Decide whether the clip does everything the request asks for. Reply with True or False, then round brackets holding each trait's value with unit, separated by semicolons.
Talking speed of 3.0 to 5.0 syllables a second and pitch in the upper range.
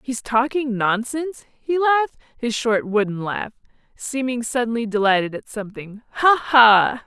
True (4.6 syllables/s; 240 Hz)